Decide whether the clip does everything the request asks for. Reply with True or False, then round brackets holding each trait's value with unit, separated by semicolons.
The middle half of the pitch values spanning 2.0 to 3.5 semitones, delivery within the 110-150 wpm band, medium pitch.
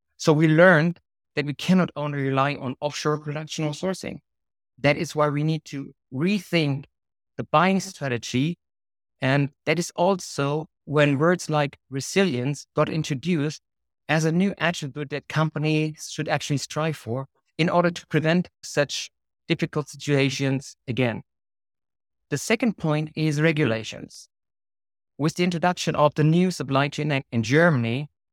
True (2.8 semitones; 140 wpm; 150 Hz)